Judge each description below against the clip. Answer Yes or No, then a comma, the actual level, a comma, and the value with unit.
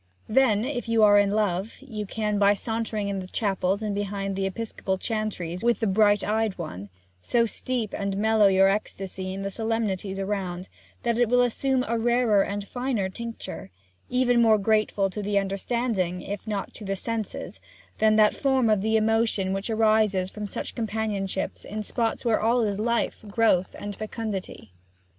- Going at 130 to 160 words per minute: No, average, 175 wpm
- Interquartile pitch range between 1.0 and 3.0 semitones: Yes, narrow, 2.6 semitones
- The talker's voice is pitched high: Yes, high, 210 Hz